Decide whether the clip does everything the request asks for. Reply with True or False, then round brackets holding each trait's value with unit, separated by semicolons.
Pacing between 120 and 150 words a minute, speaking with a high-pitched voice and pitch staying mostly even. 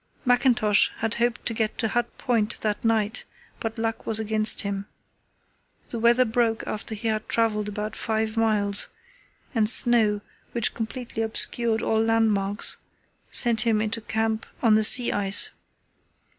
True (145 wpm; 220 Hz; 1.3 semitones)